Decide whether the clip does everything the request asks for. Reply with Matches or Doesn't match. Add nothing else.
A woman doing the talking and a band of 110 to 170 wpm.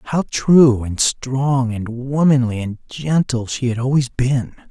Doesn't match